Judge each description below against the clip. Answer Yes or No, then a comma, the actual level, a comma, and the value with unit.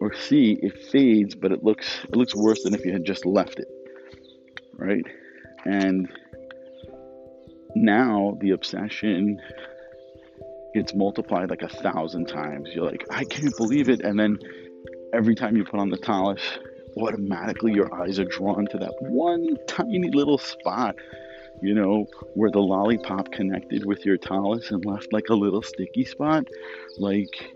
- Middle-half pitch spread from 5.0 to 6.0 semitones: Yes, wide, 5.6 semitones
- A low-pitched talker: Yes, low, 100 Hz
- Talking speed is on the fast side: No, average, 155 wpm